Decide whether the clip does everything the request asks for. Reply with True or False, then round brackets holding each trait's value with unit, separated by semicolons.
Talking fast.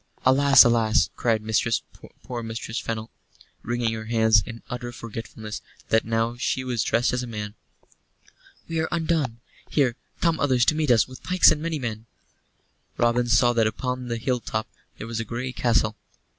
False (170 wpm)